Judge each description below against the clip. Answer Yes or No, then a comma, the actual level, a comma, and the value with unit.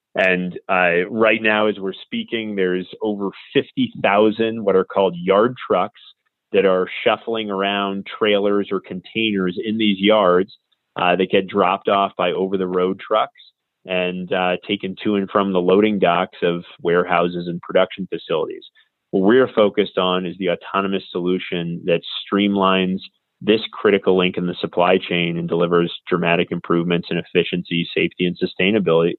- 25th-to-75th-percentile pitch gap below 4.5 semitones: Yes, average, 2.8 semitones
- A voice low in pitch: Yes, very low, 95 Hz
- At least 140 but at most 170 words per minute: Yes, average, 155 wpm